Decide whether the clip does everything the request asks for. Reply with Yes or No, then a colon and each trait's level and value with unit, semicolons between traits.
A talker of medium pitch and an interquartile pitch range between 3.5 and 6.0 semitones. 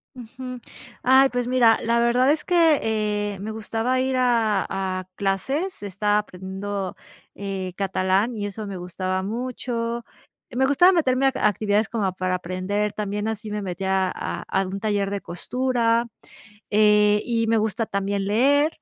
No: high, 210 Hz; average, 3.9 semitones